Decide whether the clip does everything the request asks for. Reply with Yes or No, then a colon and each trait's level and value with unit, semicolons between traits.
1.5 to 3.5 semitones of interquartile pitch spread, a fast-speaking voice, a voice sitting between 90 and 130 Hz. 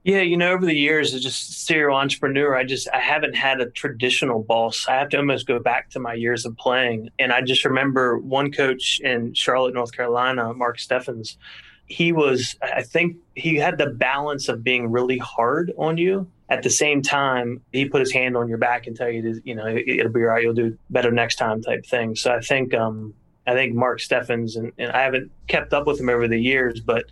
Yes: average, 2.9 semitones; fast, 225 wpm; low, 125 Hz